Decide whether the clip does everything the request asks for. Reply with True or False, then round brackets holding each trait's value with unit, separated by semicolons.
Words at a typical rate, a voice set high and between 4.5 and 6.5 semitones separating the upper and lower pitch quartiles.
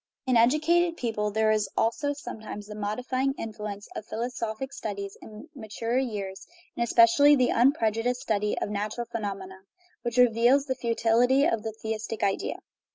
False (155 wpm; 230 Hz; 3.1 semitones)